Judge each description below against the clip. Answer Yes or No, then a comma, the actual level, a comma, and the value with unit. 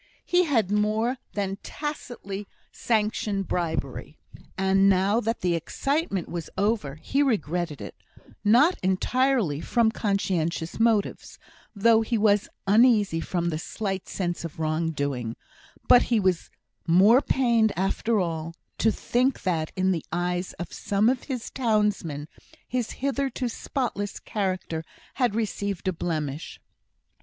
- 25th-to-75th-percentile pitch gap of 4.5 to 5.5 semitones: Yes, average, 5.0 semitones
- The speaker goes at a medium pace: No, slow, 130 wpm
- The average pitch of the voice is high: Yes, high, 200 Hz